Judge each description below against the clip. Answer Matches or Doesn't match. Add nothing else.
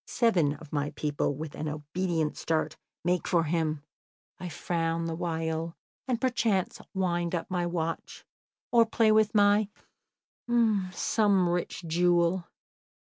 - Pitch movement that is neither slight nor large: Matches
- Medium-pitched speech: Matches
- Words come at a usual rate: Doesn't match